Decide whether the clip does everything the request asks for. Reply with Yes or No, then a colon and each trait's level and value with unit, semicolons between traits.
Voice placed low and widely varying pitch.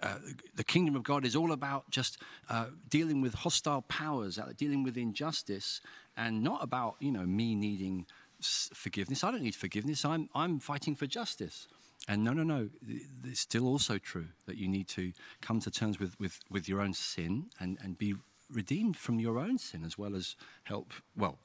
Yes: low, 115 Hz; wide, 6.3 semitones